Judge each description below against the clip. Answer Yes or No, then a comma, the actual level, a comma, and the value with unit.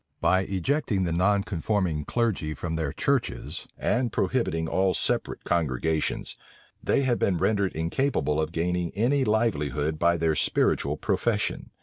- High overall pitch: No, very low, 90 Hz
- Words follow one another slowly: Yes, slow, 130 wpm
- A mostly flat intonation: No, average, 4.9 semitones